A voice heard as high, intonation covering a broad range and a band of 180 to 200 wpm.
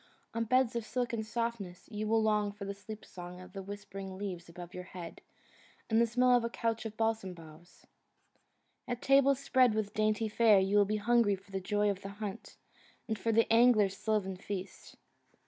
No: high, 210 Hz; average, 3.0 semitones; average, 190 wpm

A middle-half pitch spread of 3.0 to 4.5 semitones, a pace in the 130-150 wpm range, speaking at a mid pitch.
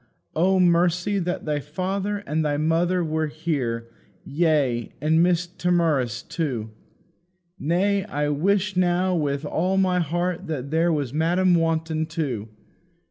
Yes: average, 3.4 semitones; slow, 135 wpm; medium, 165 Hz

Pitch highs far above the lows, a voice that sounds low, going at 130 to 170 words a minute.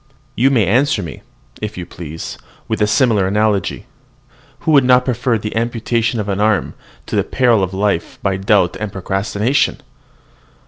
No: average, 3.5 semitones; low, 105 Hz; average, 165 wpm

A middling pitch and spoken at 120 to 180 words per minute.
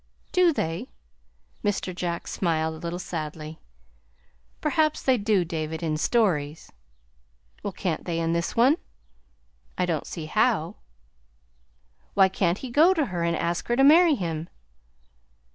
Yes: medium, 175 Hz; average, 140 wpm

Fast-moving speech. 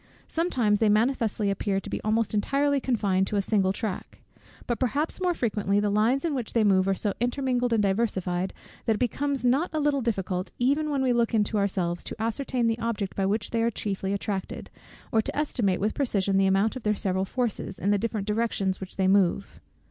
Yes: fast, 210 wpm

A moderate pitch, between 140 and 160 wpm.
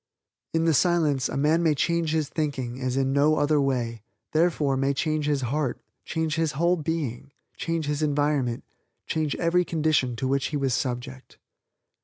No: medium, 145 Hz; average, 170 wpm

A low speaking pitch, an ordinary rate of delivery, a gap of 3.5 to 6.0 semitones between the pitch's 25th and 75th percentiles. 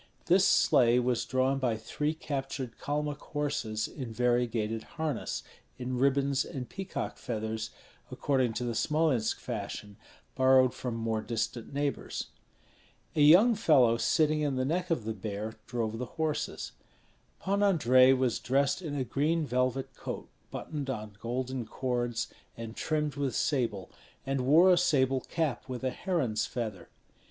Yes: low, 130 Hz; average, 145 wpm; average, 4.1 semitones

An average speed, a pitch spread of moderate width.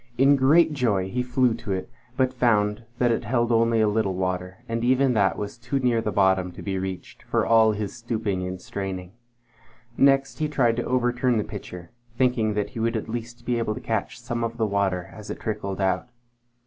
No: fast, 210 wpm; average, 3.7 semitones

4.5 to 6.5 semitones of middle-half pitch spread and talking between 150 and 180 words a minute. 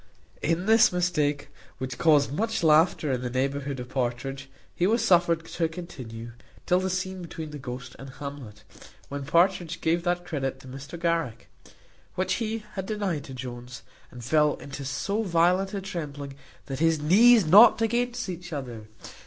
Yes: average, 5.2 semitones; average, 165 wpm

